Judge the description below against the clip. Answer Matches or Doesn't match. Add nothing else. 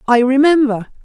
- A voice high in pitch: Matches